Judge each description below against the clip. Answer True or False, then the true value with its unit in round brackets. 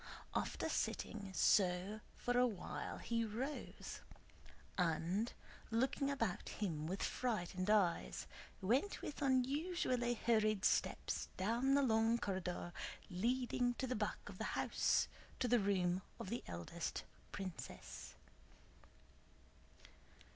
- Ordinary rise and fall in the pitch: True (4.9 semitones)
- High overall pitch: True (220 Hz)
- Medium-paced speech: False (110 wpm)